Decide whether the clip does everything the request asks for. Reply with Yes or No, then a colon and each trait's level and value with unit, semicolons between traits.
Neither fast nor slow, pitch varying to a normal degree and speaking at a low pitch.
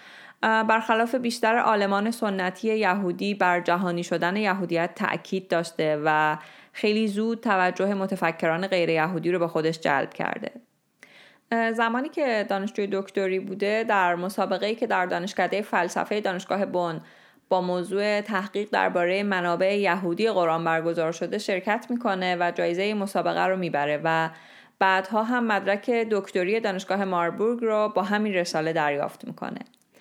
No: average, 130 wpm; average, 3.3 semitones; high, 190 Hz